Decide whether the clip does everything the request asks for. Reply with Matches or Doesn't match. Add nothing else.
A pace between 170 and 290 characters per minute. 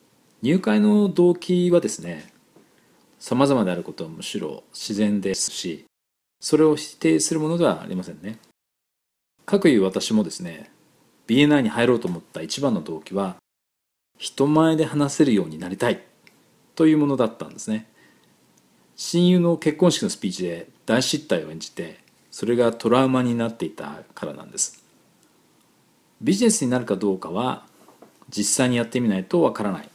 Doesn't match